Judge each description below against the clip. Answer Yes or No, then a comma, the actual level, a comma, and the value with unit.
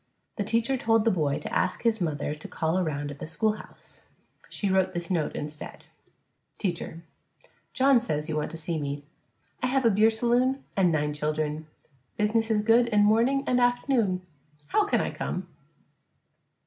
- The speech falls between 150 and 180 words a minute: Yes, average, 170 wpm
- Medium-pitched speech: No, high, 200 Hz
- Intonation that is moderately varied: No, wide, 7.0 semitones